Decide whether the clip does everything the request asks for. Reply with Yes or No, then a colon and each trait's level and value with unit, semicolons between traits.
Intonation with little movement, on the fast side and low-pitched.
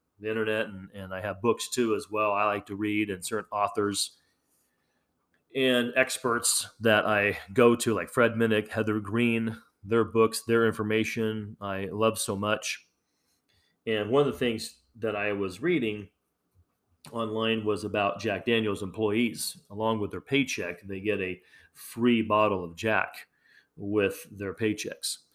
No: narrow, 2.0 semitones; average, 155 wpm; low, 110 Hz